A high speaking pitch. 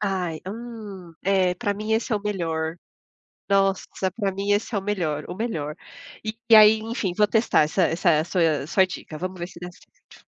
Yes: high, 195 Hz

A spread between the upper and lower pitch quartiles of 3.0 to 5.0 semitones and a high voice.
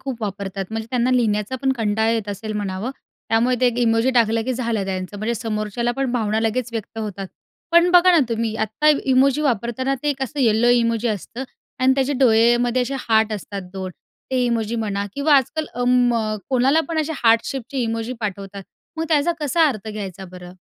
Yes: average, 3.4 semitones; high, 230 Hz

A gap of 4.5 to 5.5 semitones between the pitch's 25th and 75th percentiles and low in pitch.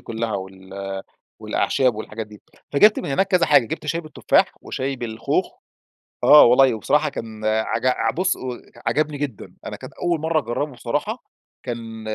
Yes: average, 5.2 semitones; low, 125 Hz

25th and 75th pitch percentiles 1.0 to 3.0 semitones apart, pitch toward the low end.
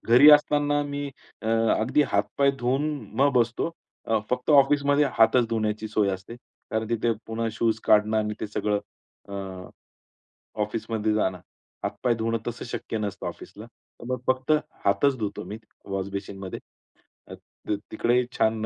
No: average, 3.5 semitones; low, 115 Hz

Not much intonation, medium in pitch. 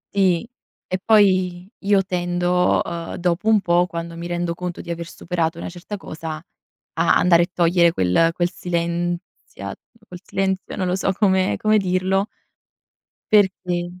Yes: narrow, 1.7 semitones; medium, 180 Hz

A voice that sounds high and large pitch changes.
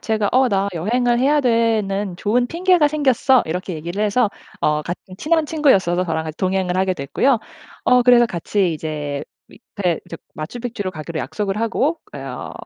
Yes: high, 205 Hz; wide, 6.0 semitones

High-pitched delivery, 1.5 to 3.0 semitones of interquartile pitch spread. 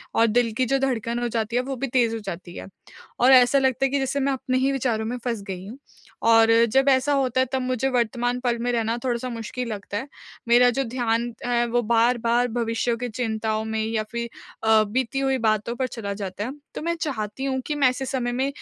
Yes: high, 240 Hz; narrow, 2.5 semitones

